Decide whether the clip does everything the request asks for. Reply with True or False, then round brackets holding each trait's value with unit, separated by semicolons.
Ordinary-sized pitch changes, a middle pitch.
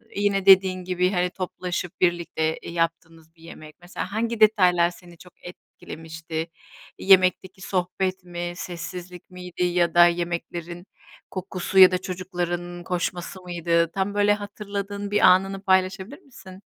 False (1.8 semitones; 180 Hz)